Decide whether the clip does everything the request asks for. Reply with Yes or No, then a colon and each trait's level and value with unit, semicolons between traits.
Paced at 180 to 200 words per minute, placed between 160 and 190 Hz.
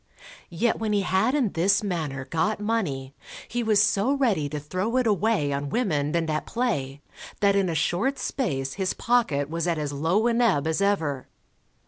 Yes: average, 185 wpm; medium, 185 Hz